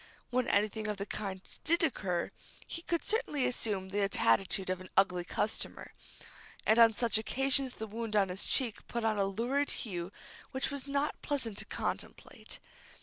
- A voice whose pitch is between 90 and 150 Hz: No, high, 220 Hz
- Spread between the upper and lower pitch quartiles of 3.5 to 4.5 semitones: No, average, 5.1 semitones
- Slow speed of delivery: No, average, 170 wpm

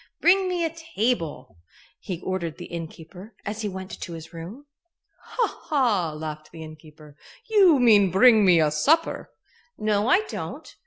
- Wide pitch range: Yes, wide, 7.6 semitones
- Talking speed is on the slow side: No, average, 155 wpm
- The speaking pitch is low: No, high, 190 Hz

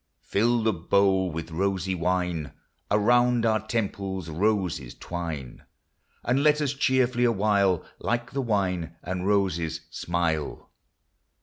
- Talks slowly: Yes, slow, 115 wpm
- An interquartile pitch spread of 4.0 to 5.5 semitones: Yes, average, 5.0 semitones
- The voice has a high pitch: No, very low, 95 Hz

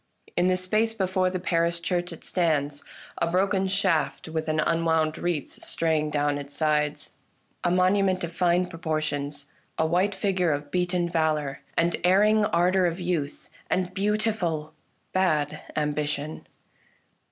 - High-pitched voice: No, medium, 170 Hz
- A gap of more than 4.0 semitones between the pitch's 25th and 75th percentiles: No, average, 3.1 semitones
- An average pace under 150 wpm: Yes, average, 140 wpm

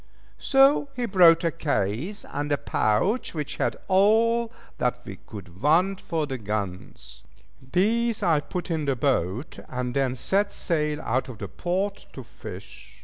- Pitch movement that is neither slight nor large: No, wide, 7.8 semitones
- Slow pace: No, average, 155 wpm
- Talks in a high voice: No, medium, 150 Hz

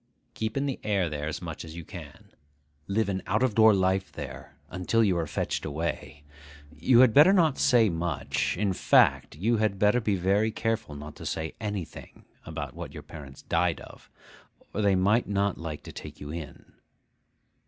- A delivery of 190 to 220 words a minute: No, average, 180 wpm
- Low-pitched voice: Yes, very low, 95 Hz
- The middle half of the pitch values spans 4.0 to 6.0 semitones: Yes, average, 5.2 semitones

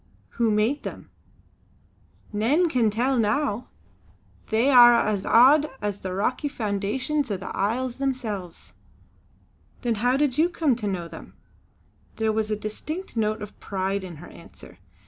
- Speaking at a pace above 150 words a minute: No, average, 145 wpm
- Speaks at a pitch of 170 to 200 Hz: No, high, 225 Hz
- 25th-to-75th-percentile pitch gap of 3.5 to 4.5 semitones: Yes, average, 4.2 semitones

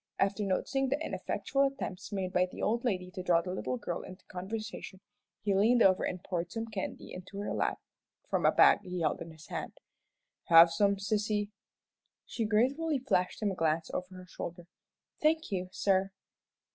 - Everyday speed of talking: Yes, average, 180 wpm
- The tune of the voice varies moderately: Yes, average, 3.4 semitones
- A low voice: No, high, 195 Hz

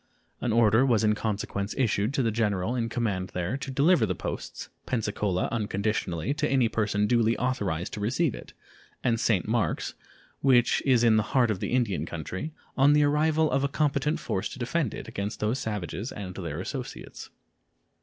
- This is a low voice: Yes, low, 115 Hz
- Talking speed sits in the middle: Yes, average, 180 wpm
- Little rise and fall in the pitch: No, average, 4.3 semitones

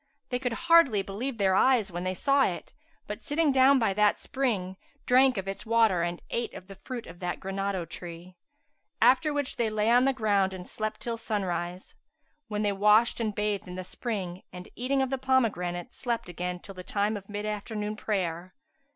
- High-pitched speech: Yes, high, 210 Hz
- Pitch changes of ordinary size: Yes, average, 4.9 semitones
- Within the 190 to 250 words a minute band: Yes, average, 200 wpm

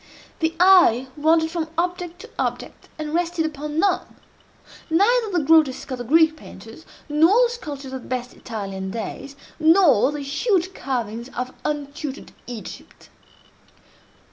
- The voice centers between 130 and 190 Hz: No, very high, 305 Hz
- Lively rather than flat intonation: No, average, 4.8 semitones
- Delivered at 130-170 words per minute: Yes, slow, 135 wpm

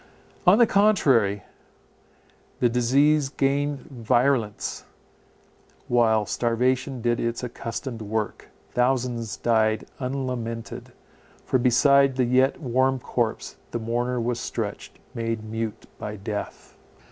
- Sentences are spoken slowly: Yes, slow, 105 wpm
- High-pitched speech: No, low, 120 Hz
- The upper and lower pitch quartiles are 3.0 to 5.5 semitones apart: No, narrow, 2.6 semitones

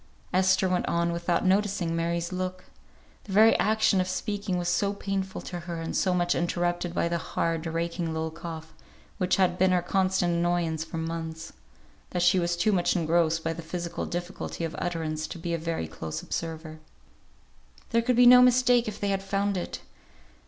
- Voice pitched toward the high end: No, medium, 175 Hz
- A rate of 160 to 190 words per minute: Yes, average, 185 wpm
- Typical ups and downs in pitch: No, narrow, 2.2 semitones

